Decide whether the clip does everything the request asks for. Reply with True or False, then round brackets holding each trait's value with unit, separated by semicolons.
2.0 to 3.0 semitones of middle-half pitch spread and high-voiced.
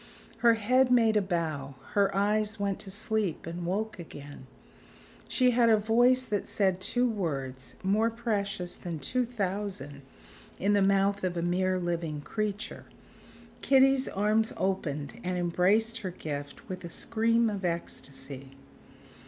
False (4.4 semitones; 200 Hz)